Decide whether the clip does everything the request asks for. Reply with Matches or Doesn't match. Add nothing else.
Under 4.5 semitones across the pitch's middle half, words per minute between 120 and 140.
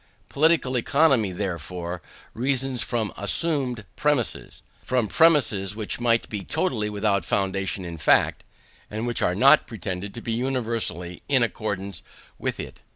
Doesn't match